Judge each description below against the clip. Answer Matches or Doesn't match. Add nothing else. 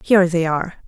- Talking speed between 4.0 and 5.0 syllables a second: Doesn't match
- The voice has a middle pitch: Matches